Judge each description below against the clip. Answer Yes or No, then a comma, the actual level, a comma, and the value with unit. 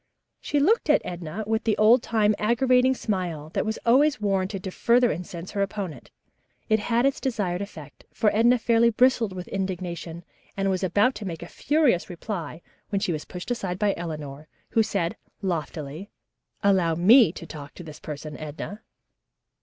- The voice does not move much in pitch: No, average, 5.0 semitones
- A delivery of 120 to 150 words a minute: No, average, 170 wpm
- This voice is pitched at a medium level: No, high, 195 Hz